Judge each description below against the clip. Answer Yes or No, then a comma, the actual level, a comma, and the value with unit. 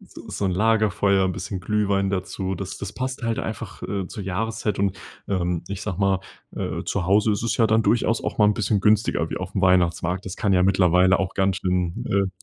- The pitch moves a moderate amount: No, narrow, 2.3 semitones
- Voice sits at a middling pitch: No, very low, 95 Hz